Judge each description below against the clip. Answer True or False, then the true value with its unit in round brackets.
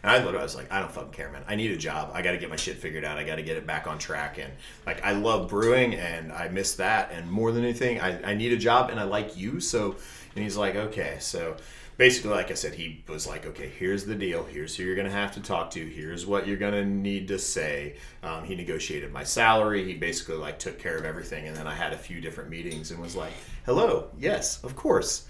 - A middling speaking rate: False (260 wpm)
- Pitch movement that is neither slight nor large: True (4.1 semitones)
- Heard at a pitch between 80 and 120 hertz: True (100 Hz)